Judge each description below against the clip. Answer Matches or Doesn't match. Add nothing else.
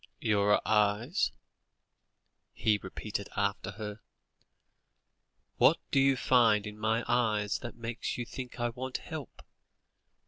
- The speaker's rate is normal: Doesn't match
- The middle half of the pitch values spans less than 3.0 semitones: Matches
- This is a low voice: Matches